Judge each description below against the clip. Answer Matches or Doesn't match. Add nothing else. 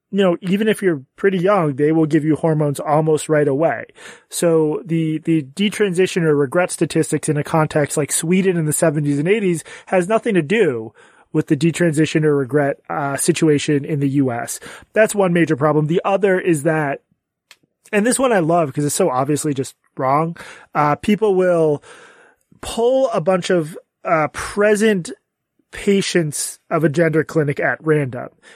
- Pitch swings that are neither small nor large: Matches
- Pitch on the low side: Doesn't match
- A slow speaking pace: Doesn't match